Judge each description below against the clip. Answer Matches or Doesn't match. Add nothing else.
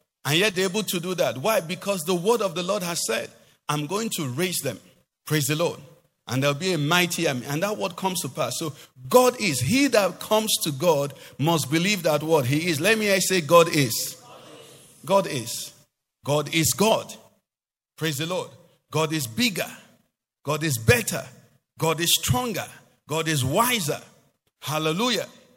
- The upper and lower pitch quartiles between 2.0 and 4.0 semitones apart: Doesn't match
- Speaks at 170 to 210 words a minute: Matches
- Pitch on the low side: Doesn't match